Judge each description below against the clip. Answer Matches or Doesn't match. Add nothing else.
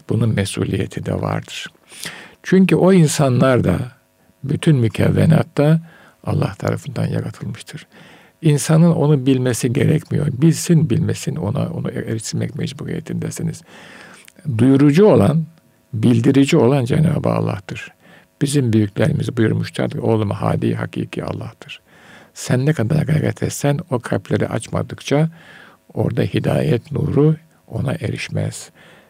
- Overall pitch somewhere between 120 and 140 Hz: Doesn't match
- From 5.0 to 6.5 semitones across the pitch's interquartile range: Doesn't match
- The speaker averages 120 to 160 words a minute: Doesn't match